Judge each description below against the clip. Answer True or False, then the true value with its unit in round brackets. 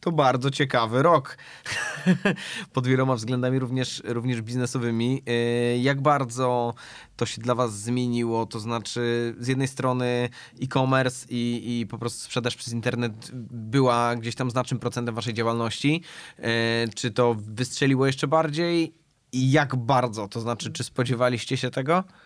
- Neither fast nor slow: True (140 wpm)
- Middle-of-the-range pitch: False (125 Hz)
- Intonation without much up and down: True (1.9 semitones)